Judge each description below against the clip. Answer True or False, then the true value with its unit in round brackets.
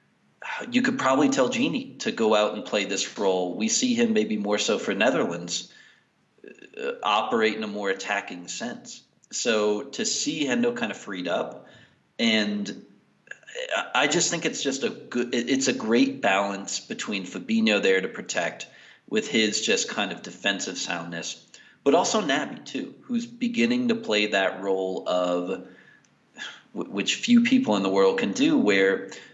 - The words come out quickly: False (160 wpm)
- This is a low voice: False (220 Hz)